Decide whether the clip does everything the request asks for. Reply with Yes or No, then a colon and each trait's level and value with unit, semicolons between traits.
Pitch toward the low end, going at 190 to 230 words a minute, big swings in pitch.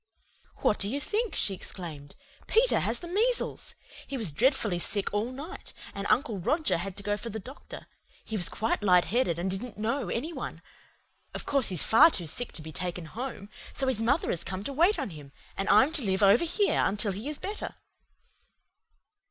No: high, 220 Hz; average, 200 wpm; wide, 6.6 semitones